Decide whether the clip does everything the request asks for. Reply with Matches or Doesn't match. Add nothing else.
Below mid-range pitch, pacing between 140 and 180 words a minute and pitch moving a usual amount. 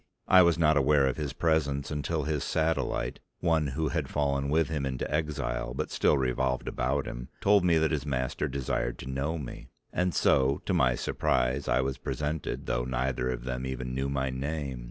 Doesn't match